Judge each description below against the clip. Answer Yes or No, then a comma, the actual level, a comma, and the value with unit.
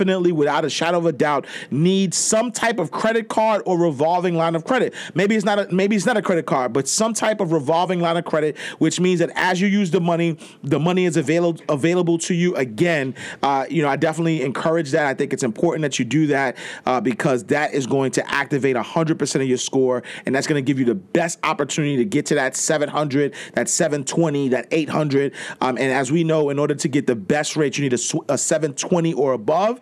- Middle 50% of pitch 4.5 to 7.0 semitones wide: No, average, 3.4 semitones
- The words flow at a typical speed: No, fast, 230 wpm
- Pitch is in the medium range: Yes, medium, 160 Hz